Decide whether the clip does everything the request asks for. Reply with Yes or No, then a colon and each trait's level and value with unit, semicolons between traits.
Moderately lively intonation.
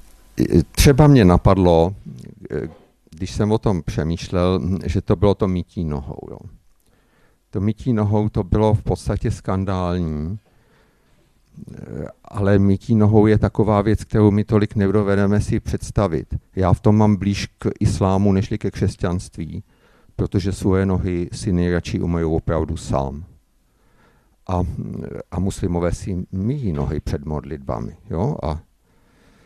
Yes: average, 3.3 semitones